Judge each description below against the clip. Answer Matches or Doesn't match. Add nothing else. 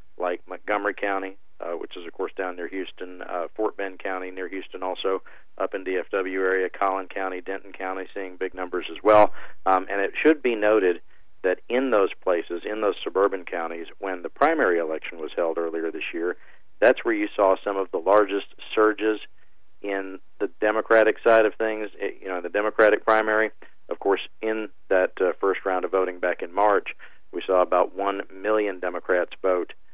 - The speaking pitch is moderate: Doesn't match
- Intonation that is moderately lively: Doesn't match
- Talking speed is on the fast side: Doesn't match